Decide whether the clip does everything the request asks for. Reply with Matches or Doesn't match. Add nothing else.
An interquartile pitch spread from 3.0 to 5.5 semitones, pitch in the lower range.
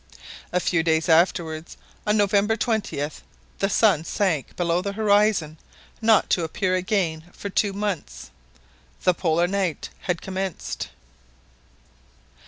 Doesn't match